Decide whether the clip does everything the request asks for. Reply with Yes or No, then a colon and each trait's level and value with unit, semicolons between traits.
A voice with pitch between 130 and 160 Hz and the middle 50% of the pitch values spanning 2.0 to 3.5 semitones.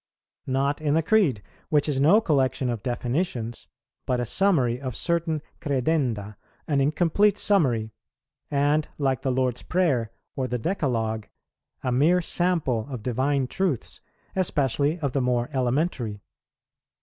No: low, 135 Hz; average, 4.5 semitones